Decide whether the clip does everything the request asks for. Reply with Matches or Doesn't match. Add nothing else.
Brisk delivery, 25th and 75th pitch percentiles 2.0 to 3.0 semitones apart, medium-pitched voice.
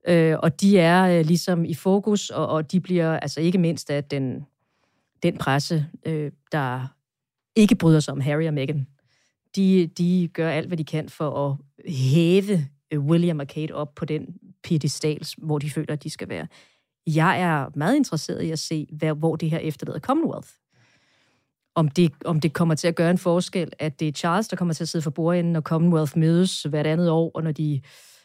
Doesn't match